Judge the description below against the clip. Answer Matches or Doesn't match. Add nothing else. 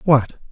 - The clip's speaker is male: Matches